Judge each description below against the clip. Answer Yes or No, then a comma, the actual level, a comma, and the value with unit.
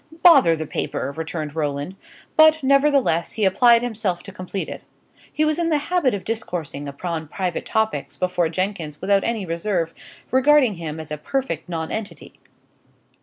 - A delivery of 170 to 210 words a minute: No, average, 155 wpm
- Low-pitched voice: No, high, 190 Hz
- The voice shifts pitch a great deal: Yes, wide, 7.5 semitones